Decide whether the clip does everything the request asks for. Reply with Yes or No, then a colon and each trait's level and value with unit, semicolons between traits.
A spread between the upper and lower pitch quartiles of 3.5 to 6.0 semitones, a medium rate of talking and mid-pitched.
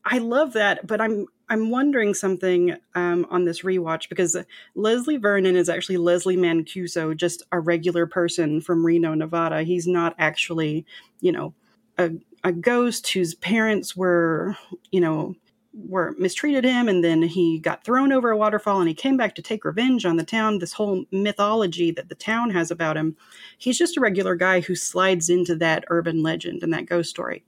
Yes: average, 4.3 semitones; average, 185 wpm; medium, 180 Hz